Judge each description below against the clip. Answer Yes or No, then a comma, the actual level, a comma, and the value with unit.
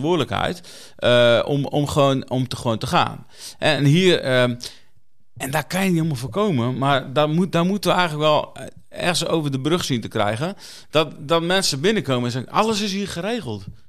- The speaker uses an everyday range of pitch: No, wide, 5.7 semitones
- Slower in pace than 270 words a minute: Yes, average, 195 wpm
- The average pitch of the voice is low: No, medium, 145 Hz